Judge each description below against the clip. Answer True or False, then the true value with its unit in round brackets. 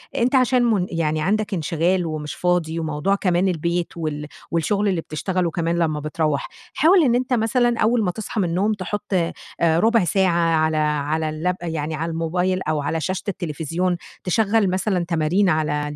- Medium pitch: True (175 Hz)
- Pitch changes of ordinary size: True (4.2 semitones)